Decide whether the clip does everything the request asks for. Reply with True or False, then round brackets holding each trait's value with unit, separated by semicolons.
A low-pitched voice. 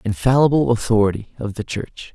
True (115 Hz)